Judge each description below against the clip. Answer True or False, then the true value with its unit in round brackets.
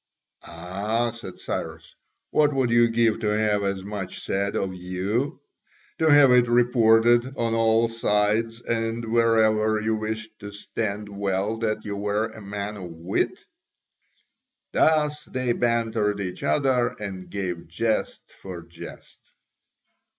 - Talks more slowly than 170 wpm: True (135 wpm)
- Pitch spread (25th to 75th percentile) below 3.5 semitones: True (2.6 semitones)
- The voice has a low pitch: True (110 Hz)